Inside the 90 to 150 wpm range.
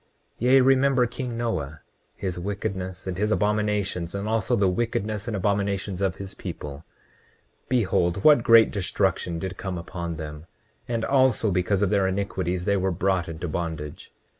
No: average, 160 wpm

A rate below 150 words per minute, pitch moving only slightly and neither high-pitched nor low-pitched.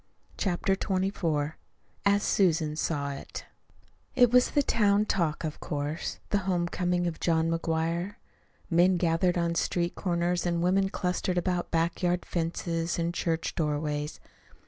Yes: average, 140 wpm; narrow, 2.1 semitones; medium, 175 Hz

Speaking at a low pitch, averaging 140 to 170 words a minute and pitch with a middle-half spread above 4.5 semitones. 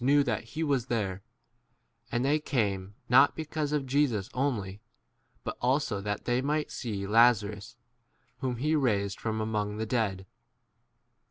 Yes: low, 120 Hz; average, 160 wpm; average, 5.2 semitones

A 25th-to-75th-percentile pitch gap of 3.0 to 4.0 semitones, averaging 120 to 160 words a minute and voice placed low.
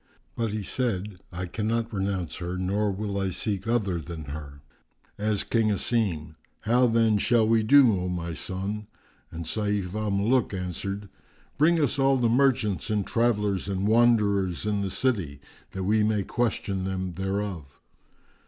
Yes: average, 3.5 semitones; average, 155 wpm; low, 100 Hz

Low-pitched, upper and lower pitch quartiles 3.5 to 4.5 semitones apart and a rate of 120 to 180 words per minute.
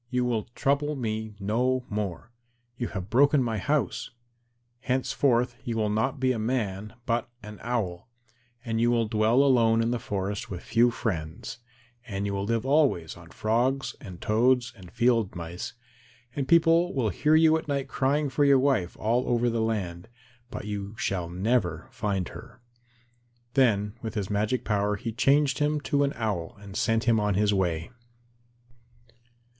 Yes: low, 115 Hz; average, 4.1 semitones; average, 165 wpm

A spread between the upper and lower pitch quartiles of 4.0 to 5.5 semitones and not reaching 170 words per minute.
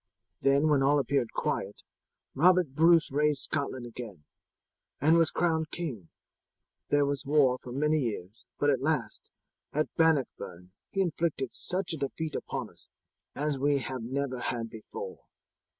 No: average, 3.5 semitones; average, 145 wpm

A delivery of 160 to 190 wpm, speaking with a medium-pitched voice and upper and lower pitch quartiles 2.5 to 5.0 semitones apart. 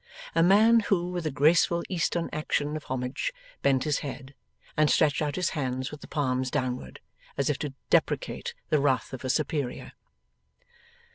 Yes: average, 165 wpm; medium, 145 Hz; average, 4.2 semitones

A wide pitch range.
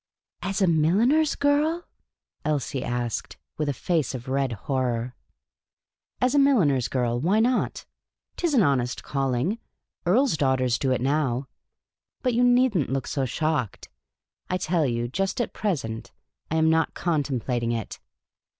Yes: wide, 8.1 semitones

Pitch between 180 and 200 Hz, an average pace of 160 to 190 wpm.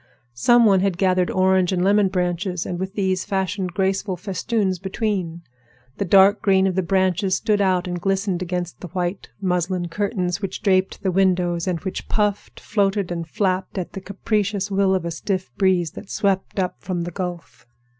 Yes: high, 190 Hz; average, 180 wpm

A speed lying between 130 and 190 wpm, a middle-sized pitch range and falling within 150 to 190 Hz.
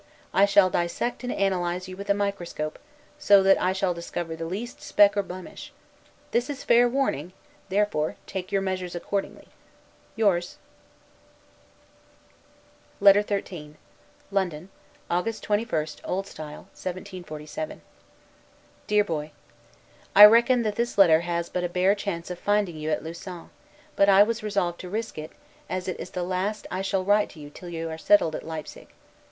Yes: average, 160 wpm; average, 3.0 semitones; medium, 185 Hz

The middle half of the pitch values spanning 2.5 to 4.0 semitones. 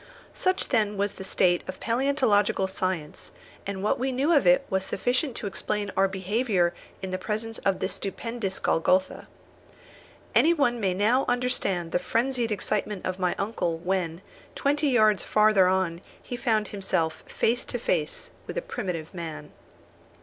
No: average, 4.5 semitones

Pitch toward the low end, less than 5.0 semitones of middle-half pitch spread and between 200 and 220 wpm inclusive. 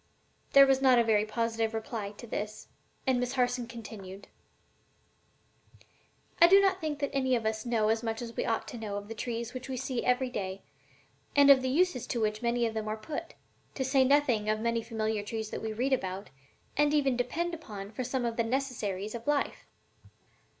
No: high, 235 Hz; average, 3.3 semitones; fast, 205 wpm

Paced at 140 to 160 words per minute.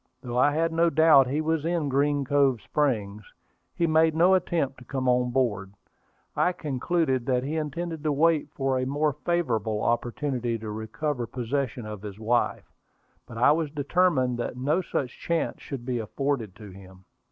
No: average, 175 wpm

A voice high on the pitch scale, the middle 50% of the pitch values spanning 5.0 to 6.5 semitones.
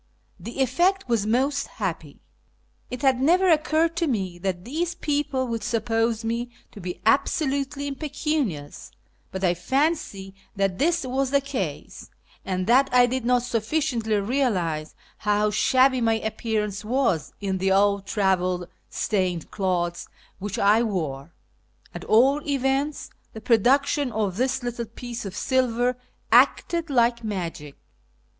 Yes: high, 235 Hz; wide, 5.6 semitones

